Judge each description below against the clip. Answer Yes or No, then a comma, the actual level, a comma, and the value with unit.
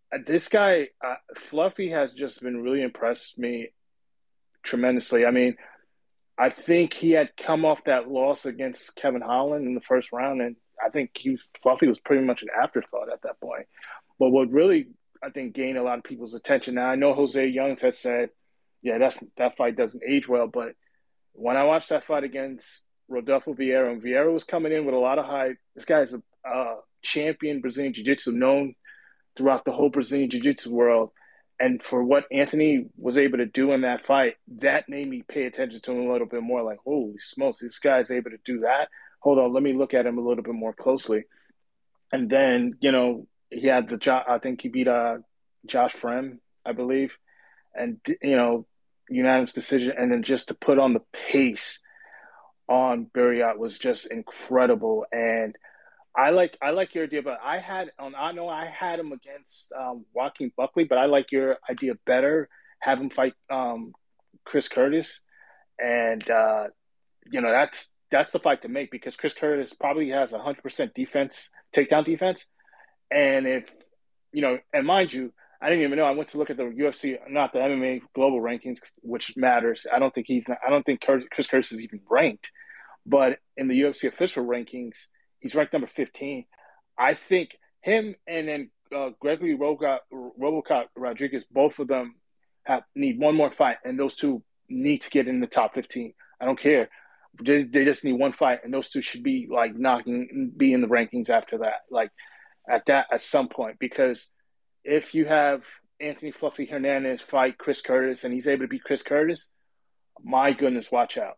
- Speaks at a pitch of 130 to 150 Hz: Yes, low, 135 Hz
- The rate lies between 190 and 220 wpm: Yes, average, 195 wpm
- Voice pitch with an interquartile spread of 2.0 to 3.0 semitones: No, average, 3.7 semitones